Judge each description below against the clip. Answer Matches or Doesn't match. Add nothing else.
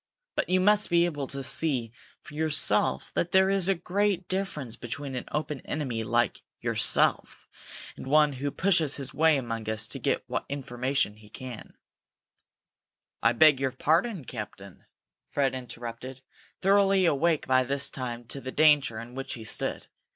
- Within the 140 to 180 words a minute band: Matches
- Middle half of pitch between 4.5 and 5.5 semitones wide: Matches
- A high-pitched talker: Doesn't match